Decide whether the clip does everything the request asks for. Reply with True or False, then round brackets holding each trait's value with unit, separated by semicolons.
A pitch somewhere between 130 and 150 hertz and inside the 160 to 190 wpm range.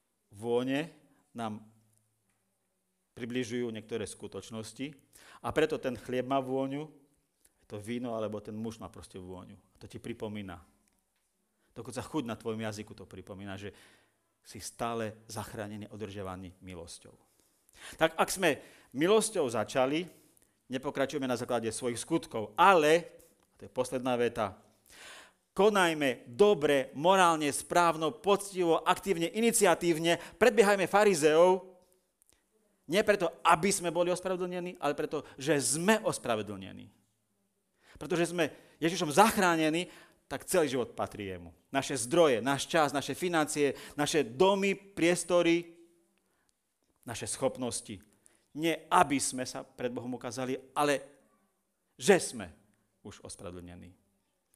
False (135 Hz; 115 wpm)